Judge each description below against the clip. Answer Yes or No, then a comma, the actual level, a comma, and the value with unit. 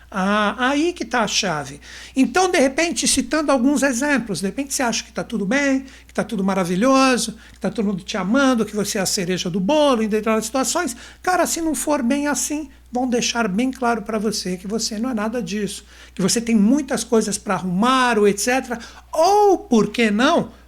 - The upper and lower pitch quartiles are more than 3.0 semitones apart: Yes, average, 4.6 semitones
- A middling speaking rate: No, fast, 205 wpm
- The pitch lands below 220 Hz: No, high, 235 Hz